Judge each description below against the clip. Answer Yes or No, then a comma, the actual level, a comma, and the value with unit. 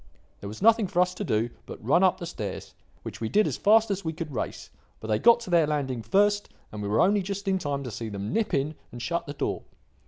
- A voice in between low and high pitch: Yes, medium, 165 Hz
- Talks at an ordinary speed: No, fast, 260 wpm